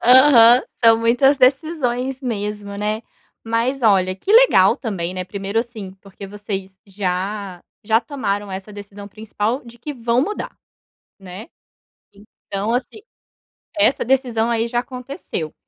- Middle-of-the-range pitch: No, high, 225 Hz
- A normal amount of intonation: Yes, average, 4.0 semitones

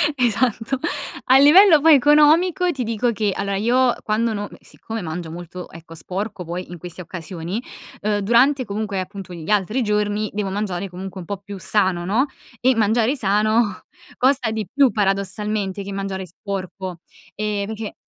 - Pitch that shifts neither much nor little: Yes, average, 3.7 semitones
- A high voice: Yes, high, 205 Hz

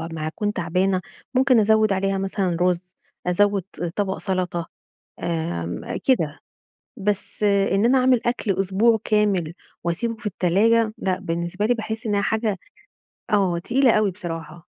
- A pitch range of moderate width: Yes, average, 3.8 semitones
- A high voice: Yes, high, 195 Hz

